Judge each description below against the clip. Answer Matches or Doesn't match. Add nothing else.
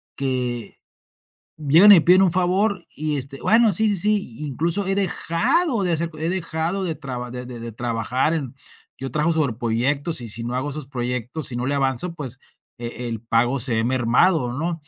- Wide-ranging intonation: Matches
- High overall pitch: Doesn't match